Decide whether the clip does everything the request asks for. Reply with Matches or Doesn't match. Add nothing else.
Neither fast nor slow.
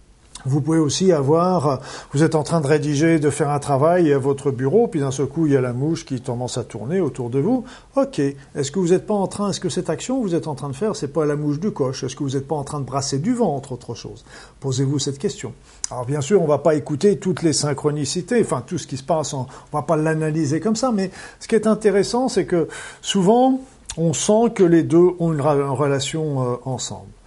Doesn't match